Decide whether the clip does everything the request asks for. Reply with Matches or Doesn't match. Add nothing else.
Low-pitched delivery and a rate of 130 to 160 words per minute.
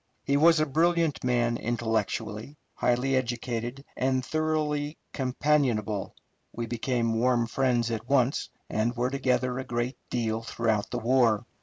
Matches